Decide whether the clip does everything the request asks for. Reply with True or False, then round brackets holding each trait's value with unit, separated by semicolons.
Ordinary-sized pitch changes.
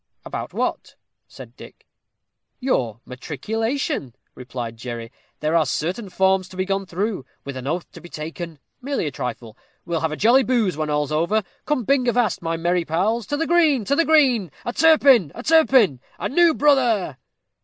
False (8.6 semitones)